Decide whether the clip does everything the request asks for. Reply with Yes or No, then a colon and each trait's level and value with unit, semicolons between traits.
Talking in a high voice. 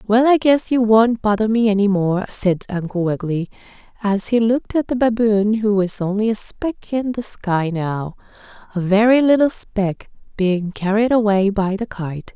Yes: high, 210 Hz